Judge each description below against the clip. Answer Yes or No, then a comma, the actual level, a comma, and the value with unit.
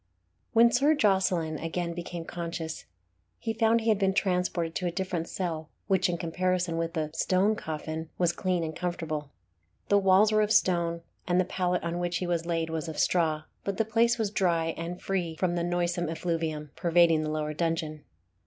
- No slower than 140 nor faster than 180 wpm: No, average, 190 wpm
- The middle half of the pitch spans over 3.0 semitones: No, narrow, 2.5 semitones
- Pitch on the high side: No, medium, 175 Hz